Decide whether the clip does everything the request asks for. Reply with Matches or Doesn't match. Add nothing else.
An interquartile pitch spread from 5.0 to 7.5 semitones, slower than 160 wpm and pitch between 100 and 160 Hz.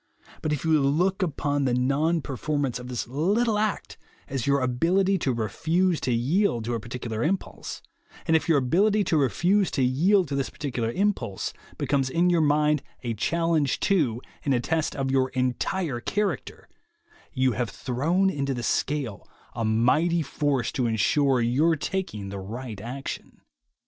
Doesn't match